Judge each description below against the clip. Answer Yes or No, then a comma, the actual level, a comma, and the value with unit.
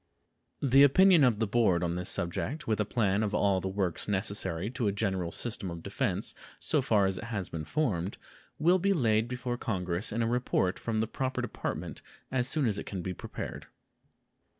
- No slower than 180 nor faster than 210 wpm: Yes, average, 195 wpm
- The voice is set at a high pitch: No, low, 105 Hz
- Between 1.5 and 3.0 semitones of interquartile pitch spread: No, average, 4.7 semitones